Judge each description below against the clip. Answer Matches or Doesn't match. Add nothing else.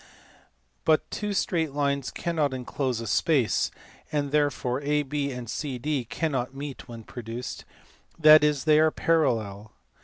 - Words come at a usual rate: Doesn't match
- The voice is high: Doesn't match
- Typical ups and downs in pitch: Matches